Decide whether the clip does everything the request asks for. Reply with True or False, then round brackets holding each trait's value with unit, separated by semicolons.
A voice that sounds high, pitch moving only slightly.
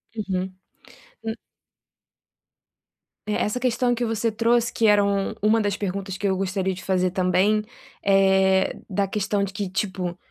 True (200 Hz; 2.1 semitones)